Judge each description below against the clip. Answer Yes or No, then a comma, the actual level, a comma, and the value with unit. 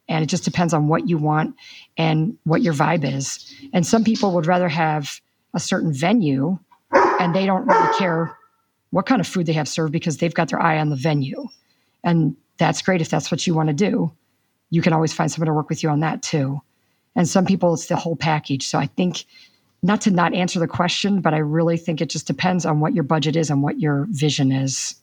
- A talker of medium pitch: Yes, medium, 165 Hz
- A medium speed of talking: No, fast, 235 wpm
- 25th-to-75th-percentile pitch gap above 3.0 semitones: No, average, 2.7 semitones